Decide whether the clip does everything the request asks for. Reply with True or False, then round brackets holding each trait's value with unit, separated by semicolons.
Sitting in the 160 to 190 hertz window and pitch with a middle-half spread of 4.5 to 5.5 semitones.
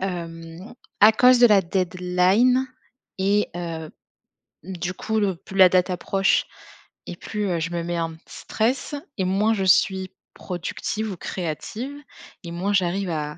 False (185 Hz; 3.2 semitones)